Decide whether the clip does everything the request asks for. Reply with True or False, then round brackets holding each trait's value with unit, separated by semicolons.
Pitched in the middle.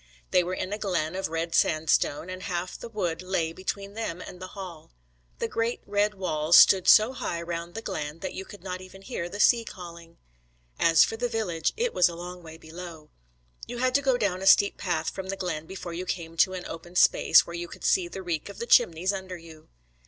True (180 Hz)